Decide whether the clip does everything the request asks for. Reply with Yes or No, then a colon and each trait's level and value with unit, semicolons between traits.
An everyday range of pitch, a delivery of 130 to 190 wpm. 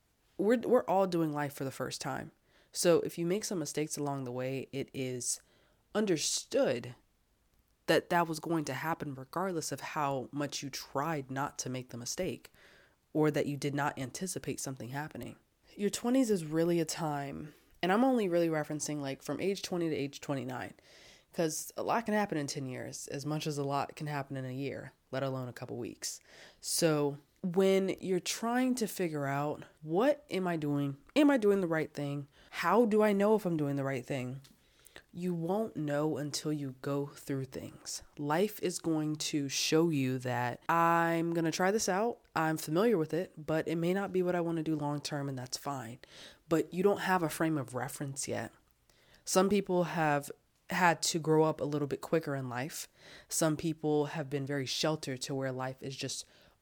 No: average, 4.0 semitones; average, 200 wpm